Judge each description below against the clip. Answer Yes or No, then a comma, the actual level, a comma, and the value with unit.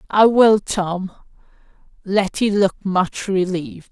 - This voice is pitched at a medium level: No, high, 195 Hz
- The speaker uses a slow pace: Yes, slow, 105 wpm